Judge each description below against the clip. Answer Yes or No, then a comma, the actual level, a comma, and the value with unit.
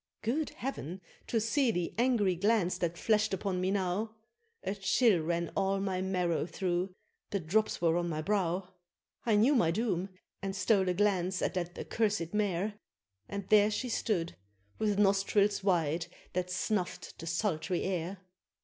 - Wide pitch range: No, average, 3.1 semitones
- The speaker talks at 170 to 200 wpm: No, average, 160 wpm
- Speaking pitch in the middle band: No, high, 195 Hz